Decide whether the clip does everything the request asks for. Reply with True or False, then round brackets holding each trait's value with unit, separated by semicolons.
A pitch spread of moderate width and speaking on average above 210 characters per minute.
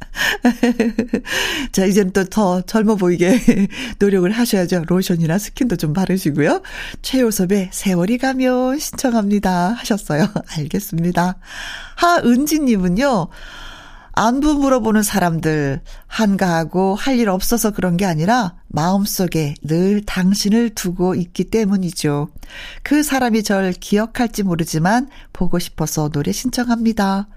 True (4.7 semitones; 270 characters per minute)